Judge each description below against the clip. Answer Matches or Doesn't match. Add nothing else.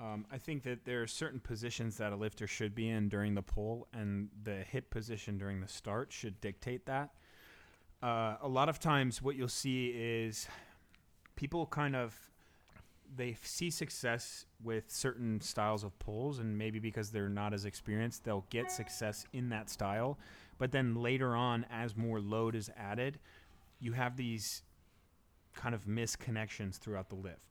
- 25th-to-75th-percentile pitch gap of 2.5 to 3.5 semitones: Matches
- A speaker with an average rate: Matches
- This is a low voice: Matches